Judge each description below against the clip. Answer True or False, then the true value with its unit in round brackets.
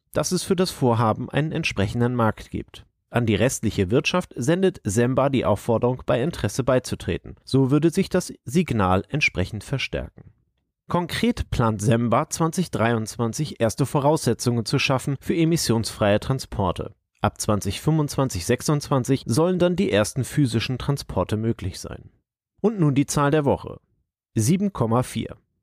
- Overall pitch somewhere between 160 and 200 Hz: False (125 Hz)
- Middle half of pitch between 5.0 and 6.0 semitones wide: True (5.3 semitones)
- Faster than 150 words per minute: False (130 wpm)